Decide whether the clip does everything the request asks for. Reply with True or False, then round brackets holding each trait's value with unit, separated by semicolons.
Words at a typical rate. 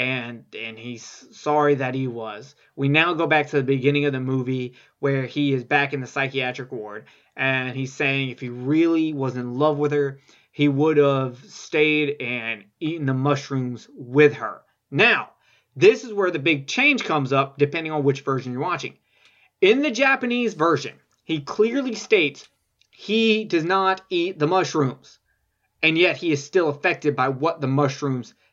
True (175 wpm)